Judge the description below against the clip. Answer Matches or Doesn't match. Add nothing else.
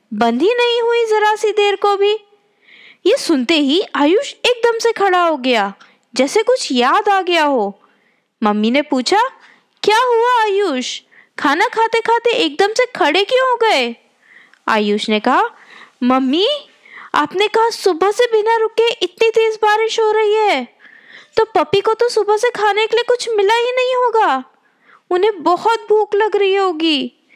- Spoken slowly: Doesn't match